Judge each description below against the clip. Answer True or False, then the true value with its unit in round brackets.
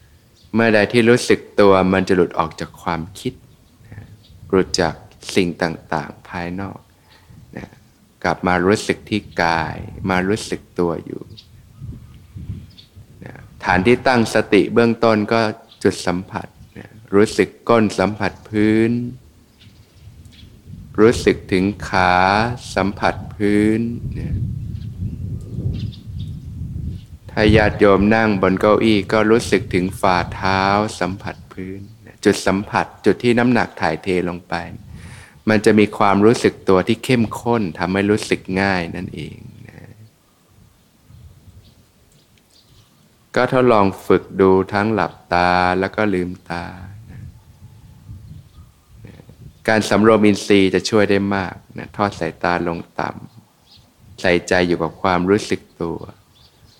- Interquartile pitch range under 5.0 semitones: True (3.2 semitones)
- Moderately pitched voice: False (105 Hz)